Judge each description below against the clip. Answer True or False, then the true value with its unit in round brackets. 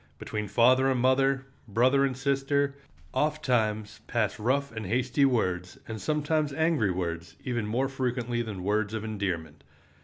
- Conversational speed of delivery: True (145 wpm)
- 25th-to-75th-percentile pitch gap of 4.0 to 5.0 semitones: True (4.4 semitones)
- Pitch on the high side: False (120 Hz)